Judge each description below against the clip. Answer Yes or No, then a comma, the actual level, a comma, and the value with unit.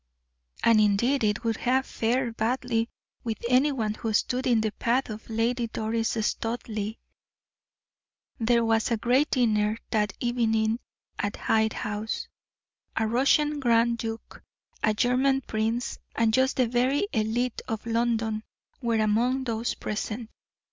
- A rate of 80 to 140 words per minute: Yes, slow, 135 wpm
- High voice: Yes, high, 230 Hz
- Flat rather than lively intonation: Yes, narrow, 2.1 semitones